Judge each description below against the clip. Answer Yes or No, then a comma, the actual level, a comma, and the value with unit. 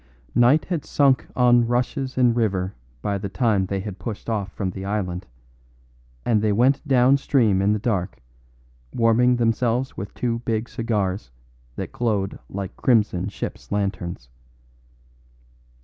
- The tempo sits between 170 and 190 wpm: No, average, 140 wpm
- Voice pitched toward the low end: Yes, low, 110 Hz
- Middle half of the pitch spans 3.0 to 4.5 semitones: Yes, average, 3.8 semitones